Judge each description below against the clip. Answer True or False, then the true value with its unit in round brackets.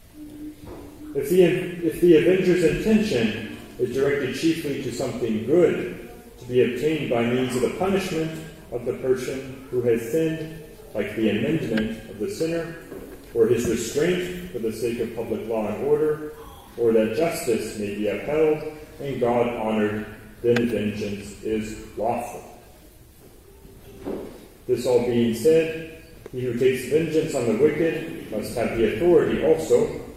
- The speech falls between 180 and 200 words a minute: False (145 wpm)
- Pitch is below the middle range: False (155 Hz)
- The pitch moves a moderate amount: False (6.5 semitones)